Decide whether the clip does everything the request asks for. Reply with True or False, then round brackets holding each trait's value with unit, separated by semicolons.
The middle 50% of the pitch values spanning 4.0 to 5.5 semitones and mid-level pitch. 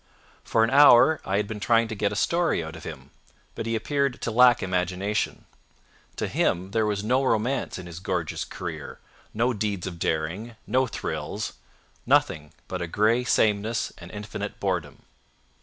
False (4.3 semitones; 105 Hz)